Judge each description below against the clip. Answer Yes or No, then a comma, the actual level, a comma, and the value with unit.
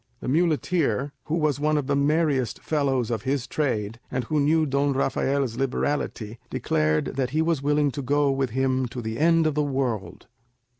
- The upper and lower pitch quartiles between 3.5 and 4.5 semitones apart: No, average, 2.8 semitones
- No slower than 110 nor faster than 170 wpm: No, average, 185 wpm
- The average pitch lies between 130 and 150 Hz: Yes, medium, 140 Hz